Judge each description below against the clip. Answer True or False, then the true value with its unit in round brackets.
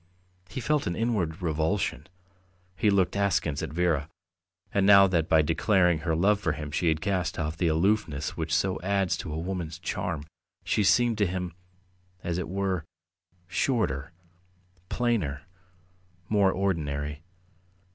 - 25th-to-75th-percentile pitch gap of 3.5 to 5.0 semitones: True (3.9 semitones)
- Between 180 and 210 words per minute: False (145 wpm)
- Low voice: True (90 Hz)